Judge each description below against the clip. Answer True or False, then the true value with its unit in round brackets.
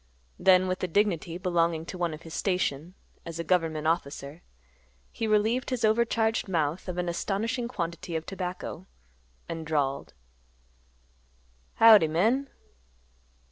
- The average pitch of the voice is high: False (180 Hz)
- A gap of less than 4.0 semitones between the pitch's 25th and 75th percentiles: False (4.3 semitones)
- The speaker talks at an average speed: False (130 wpm)